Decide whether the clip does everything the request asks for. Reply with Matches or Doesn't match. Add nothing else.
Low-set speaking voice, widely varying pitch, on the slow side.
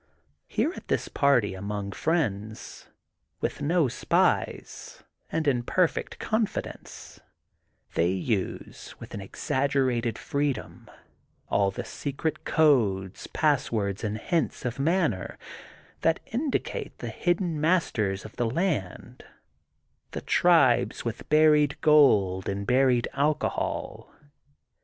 Matches